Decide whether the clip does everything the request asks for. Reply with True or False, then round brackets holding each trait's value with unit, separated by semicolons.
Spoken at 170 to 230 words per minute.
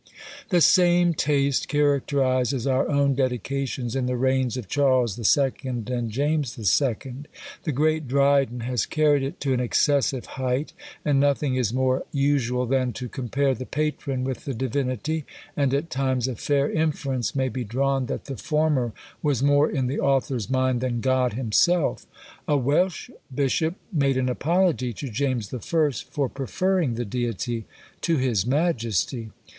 False (155 wpm)